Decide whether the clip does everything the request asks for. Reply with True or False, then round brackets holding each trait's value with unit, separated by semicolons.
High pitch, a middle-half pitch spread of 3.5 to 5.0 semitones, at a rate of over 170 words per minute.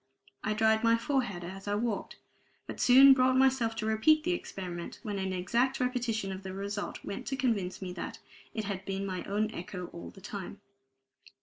True (215 Hz; 4.3 semitones; 190 wpm)